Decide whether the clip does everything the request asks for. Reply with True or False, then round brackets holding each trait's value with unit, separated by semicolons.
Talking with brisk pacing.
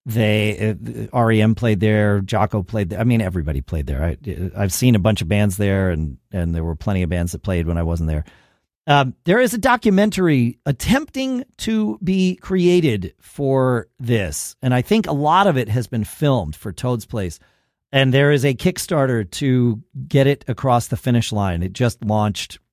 False (195 wpm)